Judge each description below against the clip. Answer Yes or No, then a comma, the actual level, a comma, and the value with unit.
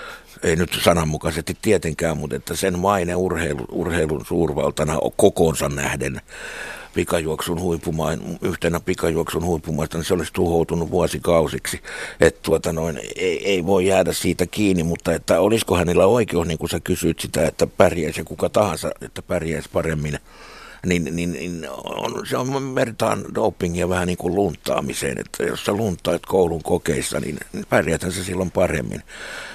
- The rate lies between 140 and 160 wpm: Yes, average, 150 wpm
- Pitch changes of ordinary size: No, narrow, 2.1 semitones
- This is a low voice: Yes, very low, 85 Hz